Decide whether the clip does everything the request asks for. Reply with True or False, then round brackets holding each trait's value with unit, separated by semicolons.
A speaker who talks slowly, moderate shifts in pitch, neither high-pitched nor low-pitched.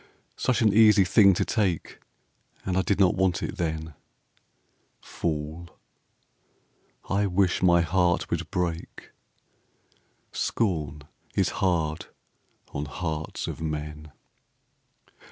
False (105 wpm; 3.7 semitones; 85 Hz)